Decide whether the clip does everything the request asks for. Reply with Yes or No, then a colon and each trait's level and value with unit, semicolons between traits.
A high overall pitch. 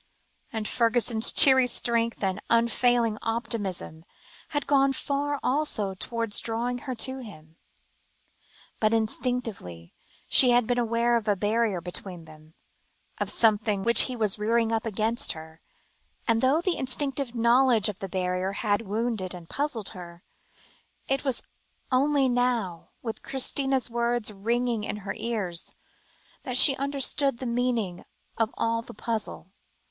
Yes: high, 230 Hz